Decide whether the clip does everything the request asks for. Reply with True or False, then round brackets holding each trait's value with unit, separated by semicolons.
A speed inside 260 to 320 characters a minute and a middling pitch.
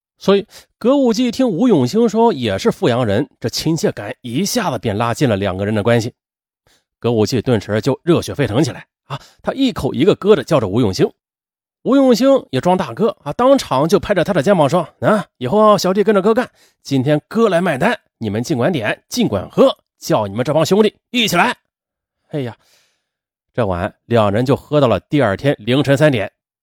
True (285 characters per minute; 155 Hz)